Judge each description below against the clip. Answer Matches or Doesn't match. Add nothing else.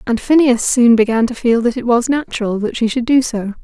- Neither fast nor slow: Doesn't match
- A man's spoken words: Doesn't match